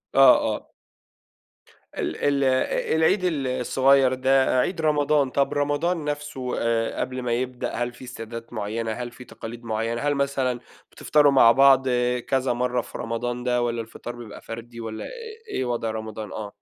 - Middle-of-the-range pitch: No, low, 125 Hz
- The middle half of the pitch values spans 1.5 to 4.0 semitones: Yes, average, 2.9 semitones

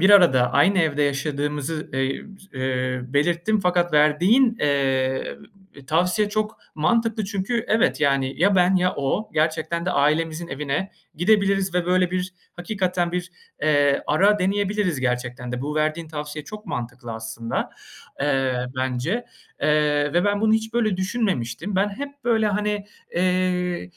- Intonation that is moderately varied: No, wide, 5.8 semitones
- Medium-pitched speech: Yes, medium, 170 Hz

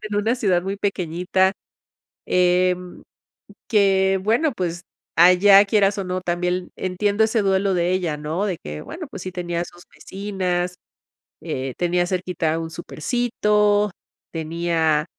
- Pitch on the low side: No, medium, 185 Hz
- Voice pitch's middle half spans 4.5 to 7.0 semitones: No, narrow, 2.6 semitones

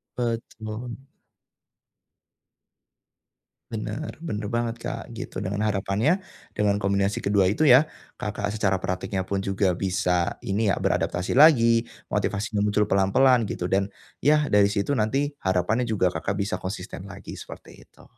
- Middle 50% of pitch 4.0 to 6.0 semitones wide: No, average, 3.0 semitones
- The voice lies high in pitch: No, low, 105 Hz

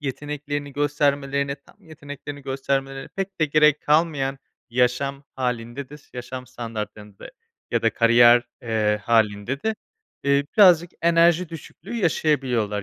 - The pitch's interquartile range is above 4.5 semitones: No, average, 3.6 semitones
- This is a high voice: No, medium, 140 Hz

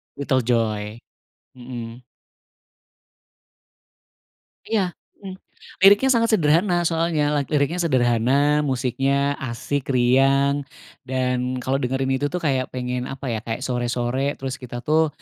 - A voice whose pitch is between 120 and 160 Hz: Yes, low, 135 Hz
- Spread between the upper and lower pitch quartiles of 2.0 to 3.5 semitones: Yes, average, 3.1 semitones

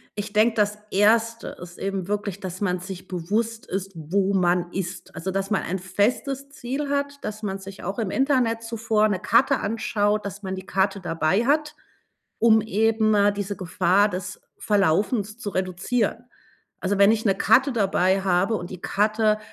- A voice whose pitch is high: Yes, high, 205 Hz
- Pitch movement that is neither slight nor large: Yes, average, 3.0 semitones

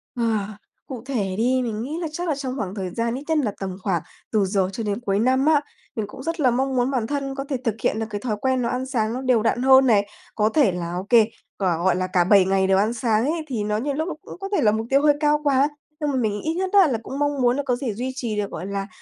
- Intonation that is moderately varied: Yes, average, 4.9 semitones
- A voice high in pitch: Yes, high, 240 Hz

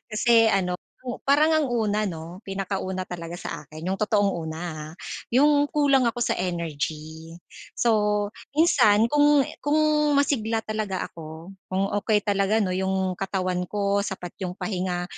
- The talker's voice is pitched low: No, high, 195 Hz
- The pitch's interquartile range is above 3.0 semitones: Yes, average, 3.8 semitones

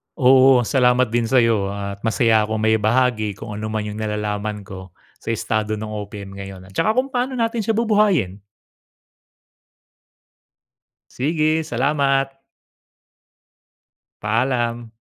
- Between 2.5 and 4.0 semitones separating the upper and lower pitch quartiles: No, average, 4.4 semitones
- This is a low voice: Yes, low, 115 Hz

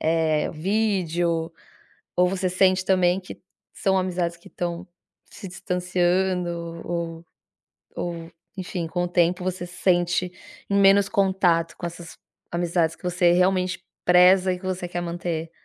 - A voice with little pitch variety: Yes, narrow, 1.5 semitones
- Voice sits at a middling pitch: Yes, medium, 180 Hz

